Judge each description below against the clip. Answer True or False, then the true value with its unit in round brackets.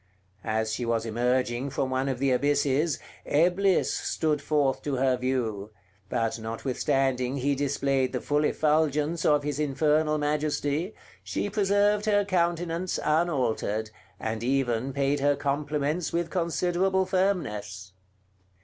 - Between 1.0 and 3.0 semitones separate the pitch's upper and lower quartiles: False (4.2 semitones)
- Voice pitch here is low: False (145 Hz)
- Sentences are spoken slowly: True (125 wpm)